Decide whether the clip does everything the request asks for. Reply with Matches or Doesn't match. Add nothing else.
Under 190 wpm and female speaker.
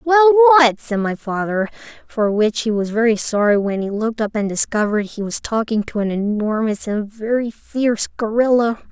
Matches